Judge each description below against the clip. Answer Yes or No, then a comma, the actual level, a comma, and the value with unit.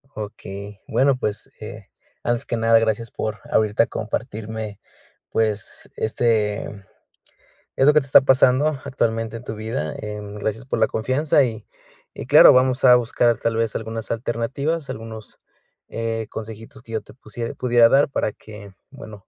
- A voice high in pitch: No, low, 115 Hz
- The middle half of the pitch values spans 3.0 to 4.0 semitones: No, narrow, 2.6 semitones